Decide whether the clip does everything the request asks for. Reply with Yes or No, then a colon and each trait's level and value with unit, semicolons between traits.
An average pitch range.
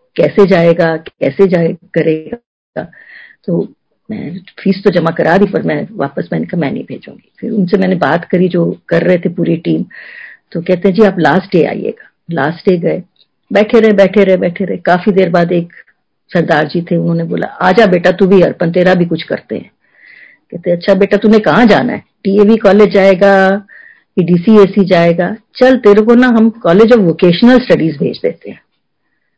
Yes: average, 3.2 semitones